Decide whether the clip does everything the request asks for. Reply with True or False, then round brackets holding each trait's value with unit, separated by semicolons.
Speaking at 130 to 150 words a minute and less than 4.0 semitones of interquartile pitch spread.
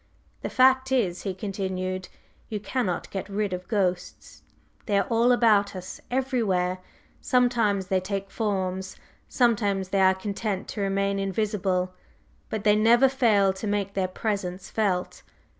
True (140 wpm; 2.7 semitones)